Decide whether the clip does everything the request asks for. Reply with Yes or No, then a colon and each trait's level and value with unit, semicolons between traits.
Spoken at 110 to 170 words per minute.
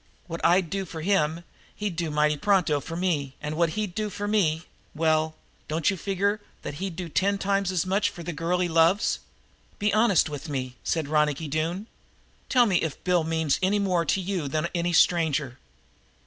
No: average, 190 wpm